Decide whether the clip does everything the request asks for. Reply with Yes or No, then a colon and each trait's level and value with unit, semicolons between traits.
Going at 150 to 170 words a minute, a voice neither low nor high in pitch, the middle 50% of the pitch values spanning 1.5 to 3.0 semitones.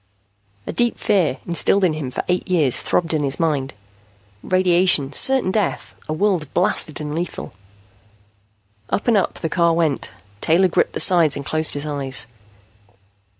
No: average, 155 wpm; medium, 165 Hz; average, 3.8 semitones